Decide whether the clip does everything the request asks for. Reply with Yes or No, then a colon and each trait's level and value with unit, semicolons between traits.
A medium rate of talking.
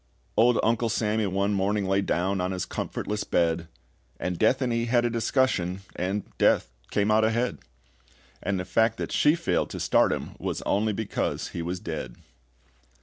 Yes: average, 175 wpm